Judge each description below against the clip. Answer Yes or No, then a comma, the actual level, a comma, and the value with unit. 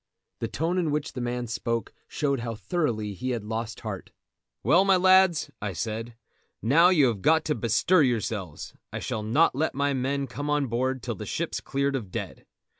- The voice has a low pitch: Yes, low, 130 Hz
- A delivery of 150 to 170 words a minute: No, average, 190 wpm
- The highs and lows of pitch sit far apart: No, average, 4.9 semitones